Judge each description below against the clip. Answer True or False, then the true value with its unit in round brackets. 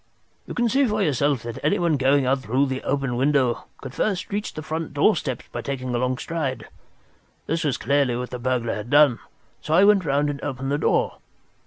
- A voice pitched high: False (140 Hz)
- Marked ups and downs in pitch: False (3.3 semitones)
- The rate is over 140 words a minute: True (200 wpm)